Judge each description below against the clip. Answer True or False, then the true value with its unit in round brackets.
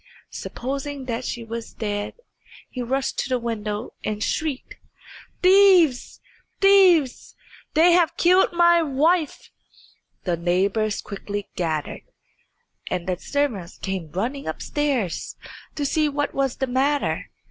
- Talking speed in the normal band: False (120 wpm)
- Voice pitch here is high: True (260 Hz)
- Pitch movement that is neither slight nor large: False (6.5 semitones)